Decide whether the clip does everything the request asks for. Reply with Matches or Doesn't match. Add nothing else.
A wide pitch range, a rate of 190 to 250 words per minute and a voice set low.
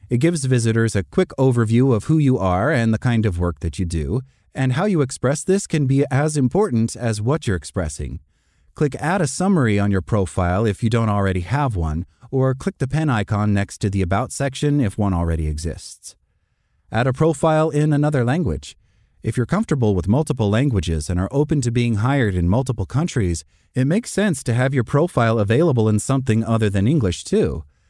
Matches